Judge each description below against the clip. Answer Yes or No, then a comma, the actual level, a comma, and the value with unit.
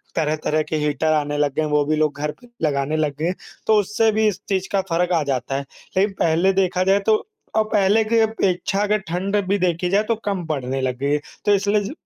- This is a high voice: No, medium, 180 Hz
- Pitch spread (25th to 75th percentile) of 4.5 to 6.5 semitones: Yes, average, 5.2 semitones